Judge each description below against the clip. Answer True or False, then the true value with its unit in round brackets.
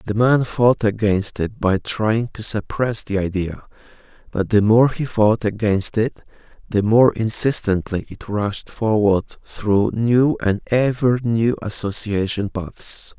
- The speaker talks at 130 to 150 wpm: True (140 wpm)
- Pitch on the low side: True (110 Hz)